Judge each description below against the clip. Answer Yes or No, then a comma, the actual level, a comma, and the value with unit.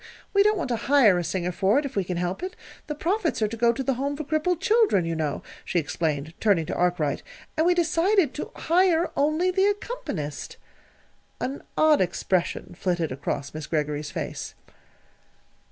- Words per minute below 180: No, average, 185 wpm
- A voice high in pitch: Yes, high, 240 Hz